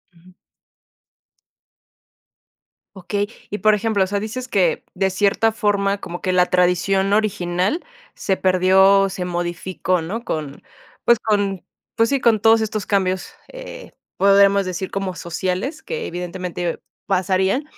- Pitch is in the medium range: No, high, 195 Hz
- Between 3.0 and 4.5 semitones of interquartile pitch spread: No, narrow, 2.6 semitones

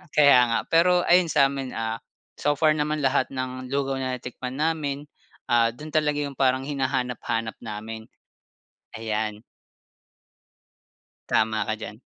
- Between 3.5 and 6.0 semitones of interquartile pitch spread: Yes, average, 4.4 semitones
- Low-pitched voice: Yes, low, 130 Hz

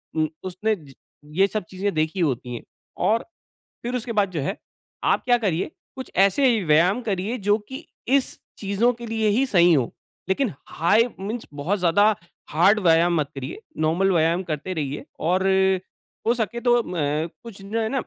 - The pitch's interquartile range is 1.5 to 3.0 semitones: No, wide, 5.4 semitones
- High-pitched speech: Yes, high, 195 Hz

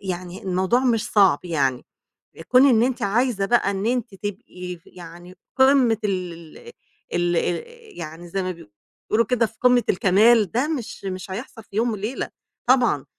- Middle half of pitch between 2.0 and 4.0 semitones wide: No, average, 5.0 semitones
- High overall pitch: Yes, high, 200 Hz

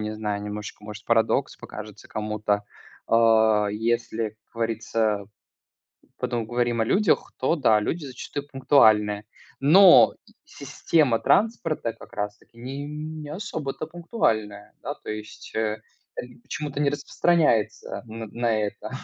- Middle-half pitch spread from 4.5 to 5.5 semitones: Yes, average, 5.2 semitones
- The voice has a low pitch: Yes, low, 115 Hz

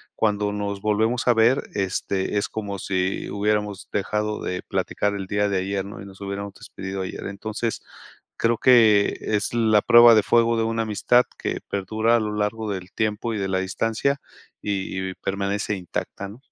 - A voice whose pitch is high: No, low, 105 Hz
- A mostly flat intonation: Yes, narrow, 2.2 semitones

